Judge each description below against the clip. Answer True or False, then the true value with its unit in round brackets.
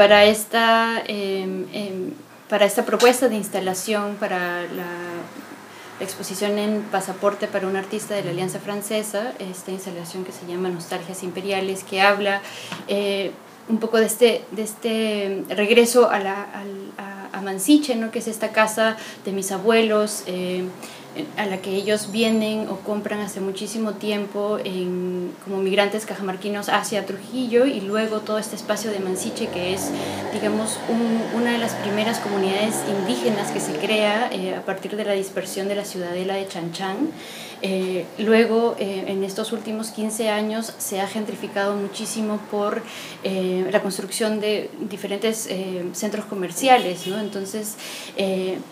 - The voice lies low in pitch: False (205 Hz)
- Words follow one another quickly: False (150 wpm)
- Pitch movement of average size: False (2.1 semitones)